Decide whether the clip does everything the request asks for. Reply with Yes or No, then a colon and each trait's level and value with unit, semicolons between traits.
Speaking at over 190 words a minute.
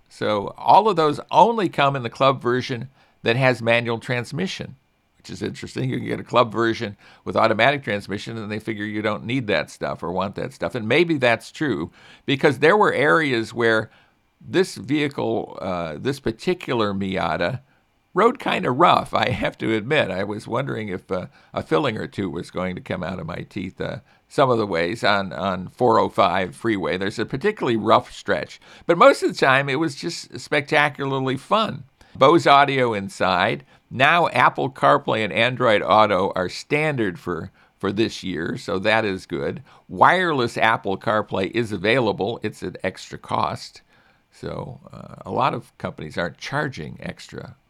No: average, 175 wpm